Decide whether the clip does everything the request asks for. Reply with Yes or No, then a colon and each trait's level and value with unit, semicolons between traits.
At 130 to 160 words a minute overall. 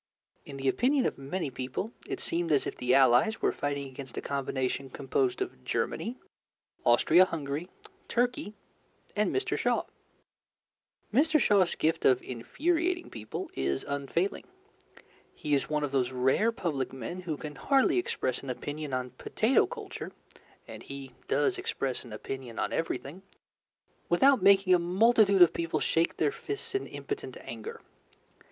Yes: average, 150 wpm